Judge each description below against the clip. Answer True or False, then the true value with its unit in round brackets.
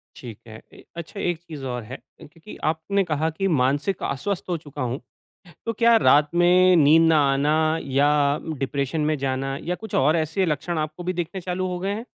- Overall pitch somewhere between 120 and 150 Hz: False (160 Hz)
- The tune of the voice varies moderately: True (4.3 semitones)